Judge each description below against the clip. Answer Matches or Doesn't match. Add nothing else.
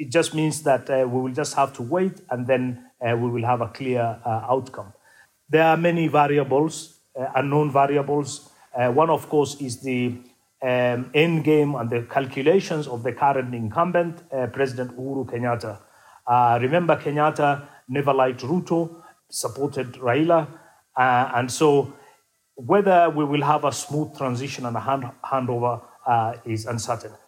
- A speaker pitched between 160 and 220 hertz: Doesn't match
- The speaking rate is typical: Matches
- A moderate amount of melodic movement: Matches